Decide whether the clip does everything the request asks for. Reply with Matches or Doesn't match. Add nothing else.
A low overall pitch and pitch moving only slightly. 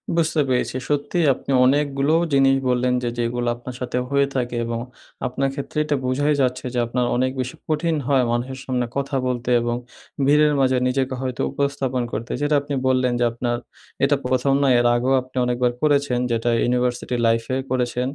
Matches